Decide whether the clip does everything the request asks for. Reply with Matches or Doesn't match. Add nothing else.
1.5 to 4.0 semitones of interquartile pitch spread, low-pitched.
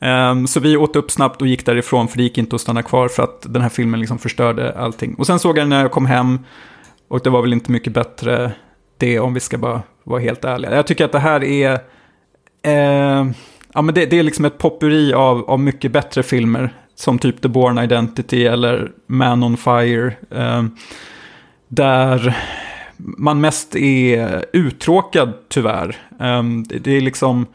Matches